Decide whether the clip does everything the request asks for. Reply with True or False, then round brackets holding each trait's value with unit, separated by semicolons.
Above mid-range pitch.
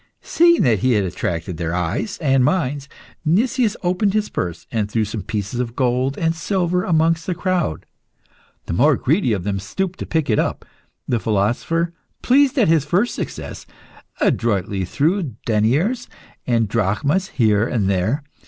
False (130 Hz)